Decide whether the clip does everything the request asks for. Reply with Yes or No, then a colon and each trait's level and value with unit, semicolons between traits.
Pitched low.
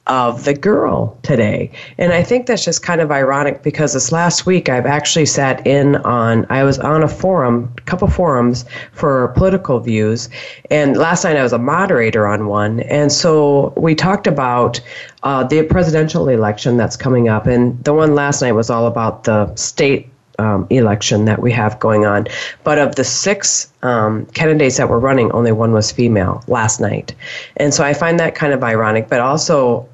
Yes: low, 130 Hz